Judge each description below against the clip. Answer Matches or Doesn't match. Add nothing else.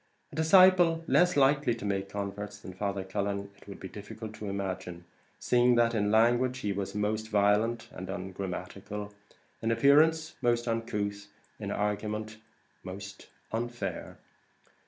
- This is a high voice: Doesn't match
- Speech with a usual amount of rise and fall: Matches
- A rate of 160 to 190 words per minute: Doesn't match